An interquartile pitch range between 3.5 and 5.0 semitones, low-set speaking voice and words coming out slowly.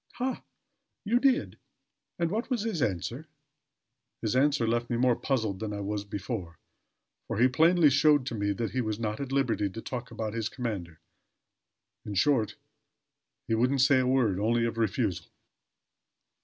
No: average, 4.7 semitones; low, 120 Hz; average, 165 wpm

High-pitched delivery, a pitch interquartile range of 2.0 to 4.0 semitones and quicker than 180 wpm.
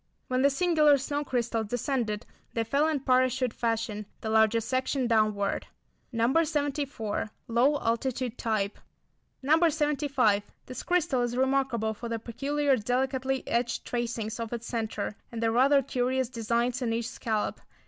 No: high, 245 Hz; average, 3.1 semitones; average, 145 wpm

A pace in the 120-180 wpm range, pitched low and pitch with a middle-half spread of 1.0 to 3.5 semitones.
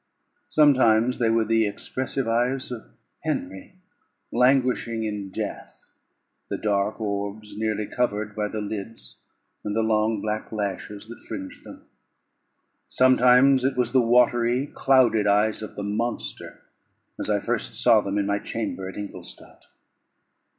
Yes: slow, 135 wpm; low, 110 Hz; average, 3.1 semitones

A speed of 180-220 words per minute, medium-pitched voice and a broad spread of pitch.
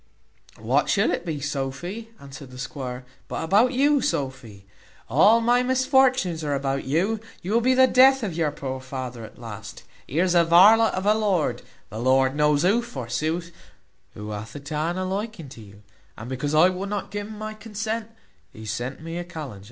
Yes: average, 190 wpm; medium, 165 Hz; wide, 8.3 semitones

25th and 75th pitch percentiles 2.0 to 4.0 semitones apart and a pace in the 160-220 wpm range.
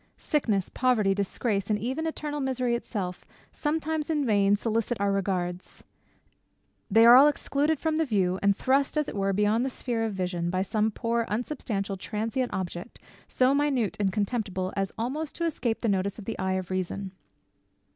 No: average, 5.0 semitones; average, 175 wpm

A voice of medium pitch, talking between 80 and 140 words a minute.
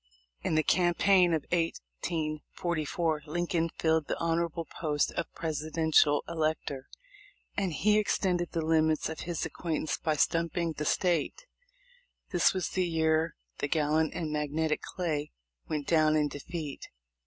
Yes: medium, 160 Hz; slow, 135 wpm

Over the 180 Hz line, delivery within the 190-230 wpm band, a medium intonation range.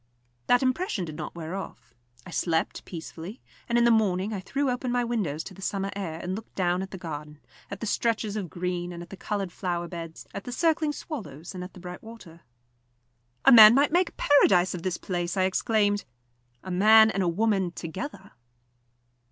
Yes: high, 190 Hz; average, 200 wpm; average, 4.4 semitones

